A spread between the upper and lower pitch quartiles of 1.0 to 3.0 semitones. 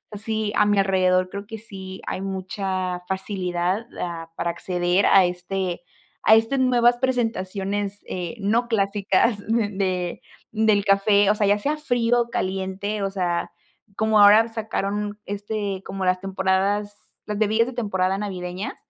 Yes: narrow, 2.4 semitones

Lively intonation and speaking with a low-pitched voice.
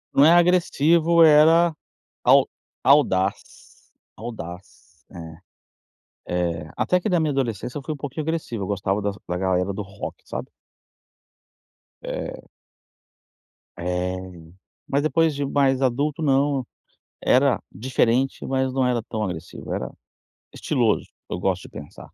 Yes: wide, 7.4 semitones; low, 130 Hz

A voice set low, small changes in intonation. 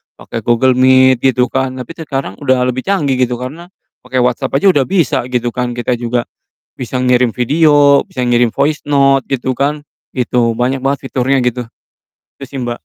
Yes: low, 130 Hz; narrow, 1.9 semitones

